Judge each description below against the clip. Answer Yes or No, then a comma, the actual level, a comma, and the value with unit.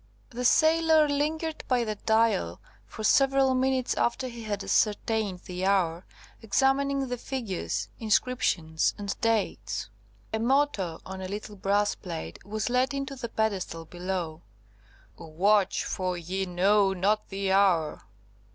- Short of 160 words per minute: Yes, slow, 135 wpm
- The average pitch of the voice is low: No, high, 210 Hz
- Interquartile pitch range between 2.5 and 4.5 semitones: No, wide, 5.4 semitones